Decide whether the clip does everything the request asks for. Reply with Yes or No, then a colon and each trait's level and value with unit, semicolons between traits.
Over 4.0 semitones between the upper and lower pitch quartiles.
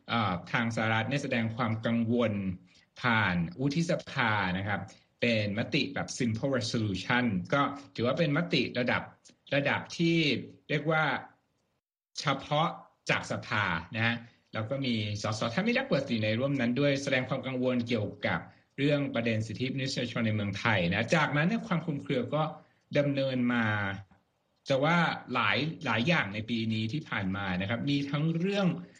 Yes: average, 4.5 semitones